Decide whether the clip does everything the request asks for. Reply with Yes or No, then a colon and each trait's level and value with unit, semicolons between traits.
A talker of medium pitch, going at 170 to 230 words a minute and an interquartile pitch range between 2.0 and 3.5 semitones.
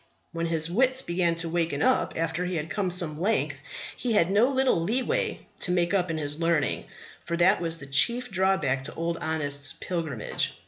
Yes: medium, 170 Hz; average, 190 wpm; average, 3.0 semitones